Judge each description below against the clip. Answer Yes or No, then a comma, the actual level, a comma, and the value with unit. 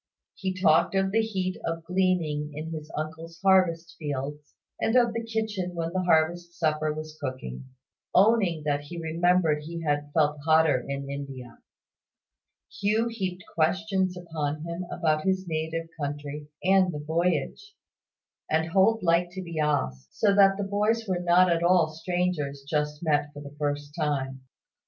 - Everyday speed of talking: Yes, average, 160 wpm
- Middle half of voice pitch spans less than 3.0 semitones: No, average, 3.7 semitones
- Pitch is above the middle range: No, medium, 165 Hz